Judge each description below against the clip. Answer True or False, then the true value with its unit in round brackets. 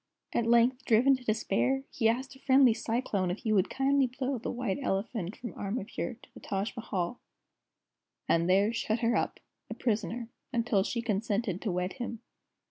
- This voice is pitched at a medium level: False (230 Hz)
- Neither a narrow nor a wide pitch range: True (3.8 semitones)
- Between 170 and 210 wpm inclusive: True (175 wpm)